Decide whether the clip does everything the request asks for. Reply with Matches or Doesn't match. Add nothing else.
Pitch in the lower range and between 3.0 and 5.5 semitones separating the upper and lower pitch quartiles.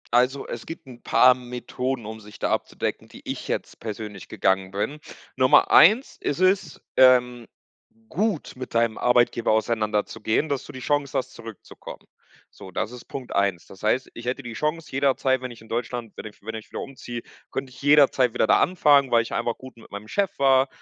Matches